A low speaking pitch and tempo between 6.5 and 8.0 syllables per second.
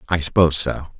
Yes: very low, 80 Hz; 6.9 syllables/s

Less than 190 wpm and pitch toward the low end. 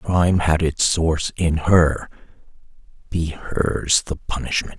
Yes: average, 140 wpm; very low, 80 Hz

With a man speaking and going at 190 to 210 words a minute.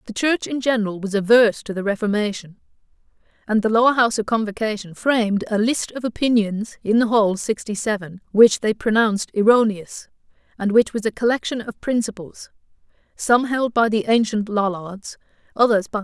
No: female; average, 200 wpm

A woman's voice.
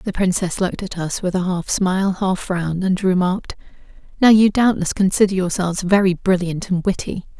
Yes: female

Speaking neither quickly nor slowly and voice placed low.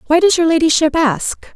No: average, 195 wpm; very high, 315 Hz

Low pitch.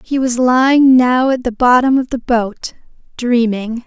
No: high, 245 Hz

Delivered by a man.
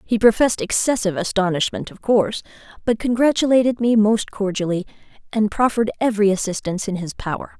No: female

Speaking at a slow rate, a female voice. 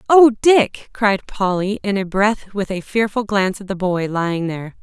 No: average, 200 wpm; female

